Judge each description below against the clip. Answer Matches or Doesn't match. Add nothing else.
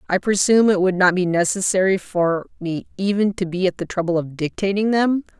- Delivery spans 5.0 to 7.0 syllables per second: Matches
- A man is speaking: Doesn't match